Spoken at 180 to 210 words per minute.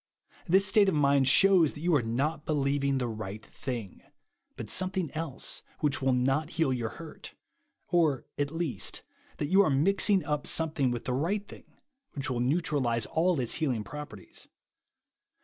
No: average, 170 wpm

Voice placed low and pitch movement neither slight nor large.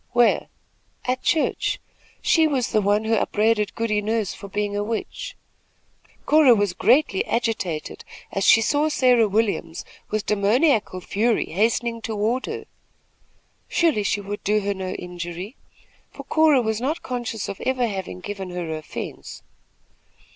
No: high, 215 Hz; average, 3.4 semitones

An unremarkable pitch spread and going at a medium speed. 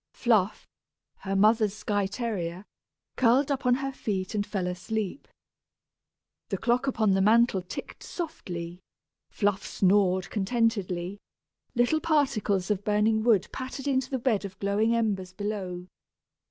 No: average, 3.9 semitones; slow, 130 wpm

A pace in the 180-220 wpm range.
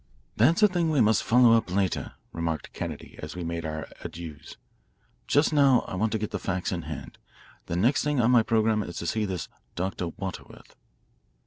Yes: average, 195 wpm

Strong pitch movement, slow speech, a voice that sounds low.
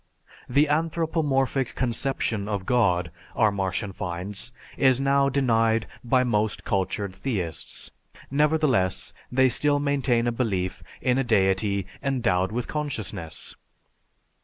Yes: wide, 5.7 semitones; slow, 110 wpm; low, 120 Hz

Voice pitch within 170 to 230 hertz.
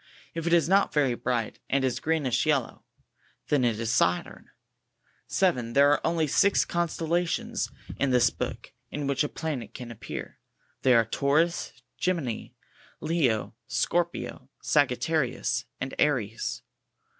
No: medium, 140 Hz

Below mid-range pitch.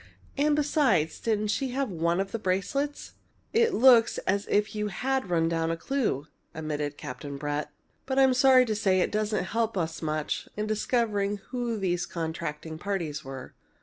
No: high, 200 Hz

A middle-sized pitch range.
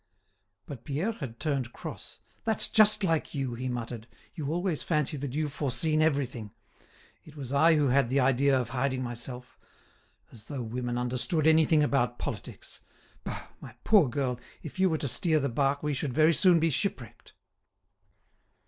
Yes: average, 3.9 semitones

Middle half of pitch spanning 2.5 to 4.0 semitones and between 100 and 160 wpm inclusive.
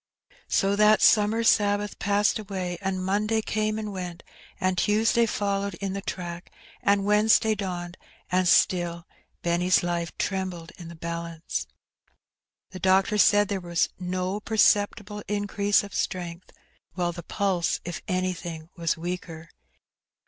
Yes: average, 2.9 semitones; slow, 135 wpm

